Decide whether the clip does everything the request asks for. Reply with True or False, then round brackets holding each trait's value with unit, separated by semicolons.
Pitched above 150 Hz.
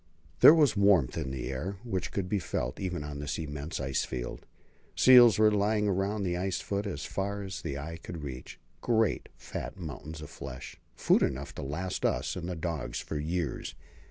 False (85 Hz)